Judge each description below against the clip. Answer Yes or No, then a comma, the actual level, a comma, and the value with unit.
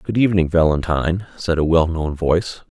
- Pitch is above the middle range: No, very low, 85 Hz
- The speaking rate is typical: Yes, average, 155 wpm